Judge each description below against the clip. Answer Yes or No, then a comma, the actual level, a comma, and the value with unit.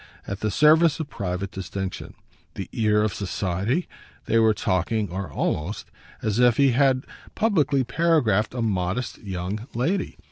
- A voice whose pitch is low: Yes, low, 110 Hz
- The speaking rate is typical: Yes, average, 145 wpm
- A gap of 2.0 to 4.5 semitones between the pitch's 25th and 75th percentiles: No, wide, 5.6 semitones